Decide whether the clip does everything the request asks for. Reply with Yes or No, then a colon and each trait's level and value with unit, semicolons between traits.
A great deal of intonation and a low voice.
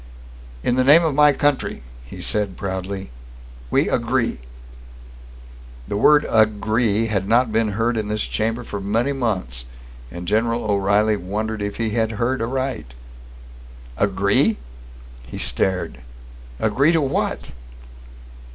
No: average, 3.3 semitones; low, 110 Hz